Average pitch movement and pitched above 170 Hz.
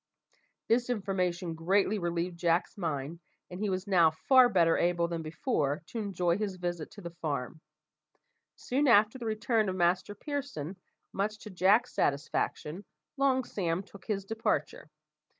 Yes: average, 4.1 semitones; medium, 185 Hz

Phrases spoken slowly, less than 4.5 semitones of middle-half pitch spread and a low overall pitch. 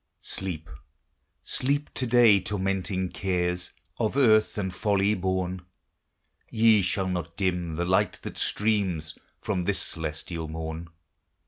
Yes: slow, 120 wpm; average, 3.1 semitones; very low, 95 Hz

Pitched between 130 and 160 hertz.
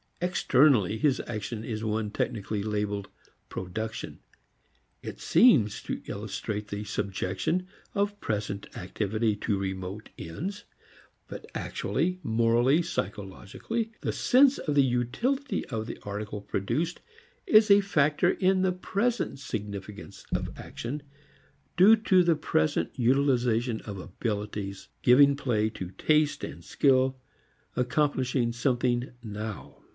No: low, 120 Hz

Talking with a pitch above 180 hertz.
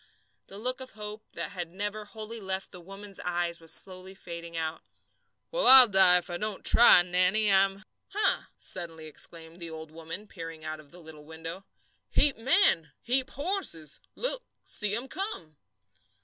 Yes: high, 190 Hz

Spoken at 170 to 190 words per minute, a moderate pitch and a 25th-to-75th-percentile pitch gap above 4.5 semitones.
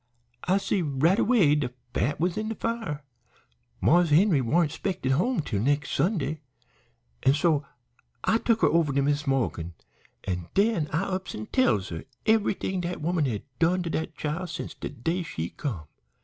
Yes: average, 175 wpm; medium, 160 Hz; average, 5.2 semitones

